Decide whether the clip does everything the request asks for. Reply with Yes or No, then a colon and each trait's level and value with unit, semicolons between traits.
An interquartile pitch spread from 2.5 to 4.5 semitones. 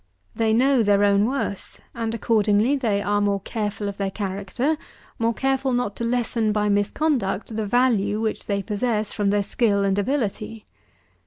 Yes: average, 2.8 semitones